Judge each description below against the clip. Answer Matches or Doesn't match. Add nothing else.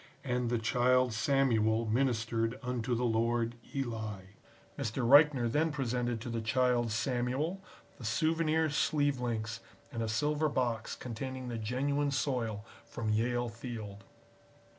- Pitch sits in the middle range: Doesn't match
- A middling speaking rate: Doesn't match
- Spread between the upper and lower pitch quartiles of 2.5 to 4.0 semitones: Matches